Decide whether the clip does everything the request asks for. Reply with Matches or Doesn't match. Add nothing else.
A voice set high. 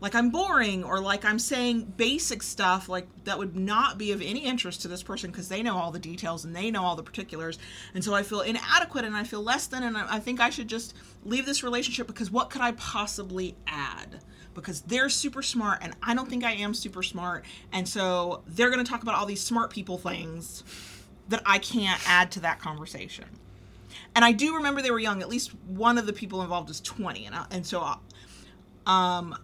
Matches